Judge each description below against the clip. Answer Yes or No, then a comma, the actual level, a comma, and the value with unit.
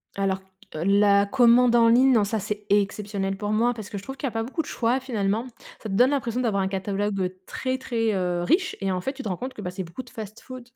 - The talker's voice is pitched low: No, high, 215 Hz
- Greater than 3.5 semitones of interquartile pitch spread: Yes, average, 4.0 semitones